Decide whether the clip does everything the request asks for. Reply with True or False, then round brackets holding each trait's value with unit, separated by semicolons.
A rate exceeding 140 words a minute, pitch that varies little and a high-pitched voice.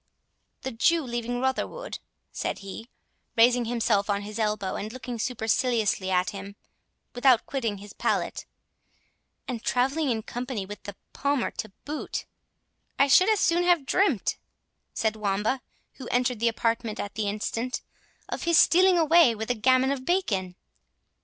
False (150 wpm; 4.0 semitones; 240 Hz)